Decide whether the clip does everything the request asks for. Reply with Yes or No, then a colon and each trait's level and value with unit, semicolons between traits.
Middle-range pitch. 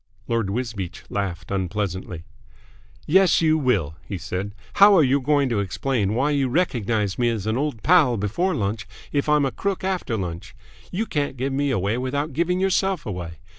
No: low, 125 Hz